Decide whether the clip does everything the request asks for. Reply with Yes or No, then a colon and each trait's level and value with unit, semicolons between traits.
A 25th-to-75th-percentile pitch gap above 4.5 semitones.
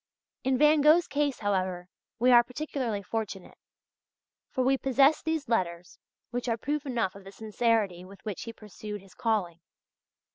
Yes: average, 5.3 semitones